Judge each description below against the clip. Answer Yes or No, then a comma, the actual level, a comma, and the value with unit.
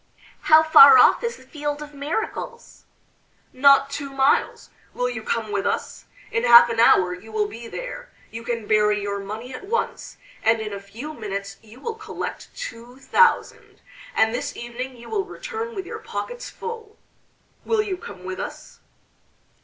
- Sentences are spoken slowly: No, average, 170 wpm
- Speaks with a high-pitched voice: Yes, very high, 250 Hz